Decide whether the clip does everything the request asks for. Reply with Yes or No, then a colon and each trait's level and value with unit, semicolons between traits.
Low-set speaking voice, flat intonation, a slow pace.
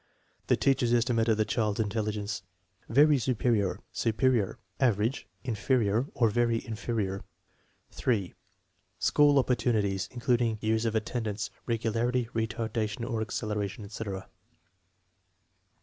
Yes: low, 115 Hz; narrow, 2.3 semitones; slow, 115 wpm